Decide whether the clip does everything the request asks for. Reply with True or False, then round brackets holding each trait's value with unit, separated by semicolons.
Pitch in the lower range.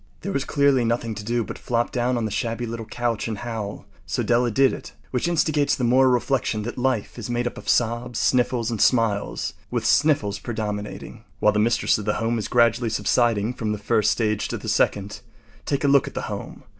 True (120 Hz)